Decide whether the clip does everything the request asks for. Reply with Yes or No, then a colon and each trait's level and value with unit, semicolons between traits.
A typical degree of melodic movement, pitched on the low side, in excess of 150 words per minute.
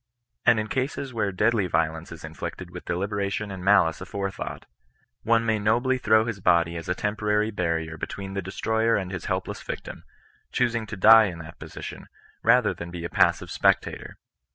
Yes: average, 4.1 semitones; low, 100 Hz; average, 180 wpm